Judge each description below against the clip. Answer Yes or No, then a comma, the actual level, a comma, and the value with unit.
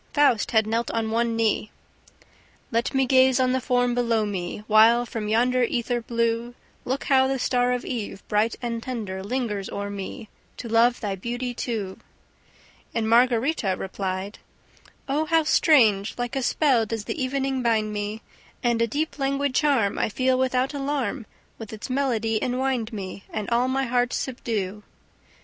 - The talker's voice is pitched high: Yes, high, 235 Hz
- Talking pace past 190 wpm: No, average, 165 wpm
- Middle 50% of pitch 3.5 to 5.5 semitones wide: No, average, 3.1 semitones